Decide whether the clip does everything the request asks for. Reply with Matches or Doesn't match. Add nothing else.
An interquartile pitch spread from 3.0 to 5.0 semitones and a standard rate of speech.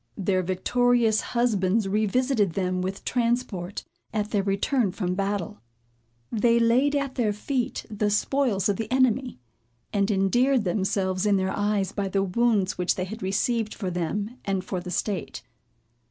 Matches